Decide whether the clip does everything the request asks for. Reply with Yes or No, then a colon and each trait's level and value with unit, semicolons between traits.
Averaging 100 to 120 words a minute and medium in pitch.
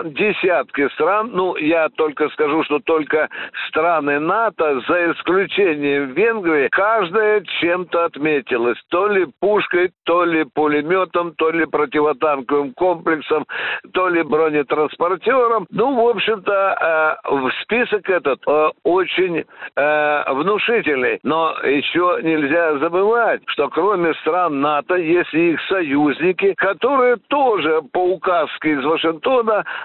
Yes: average, 115 wpm; medium, 170 Hz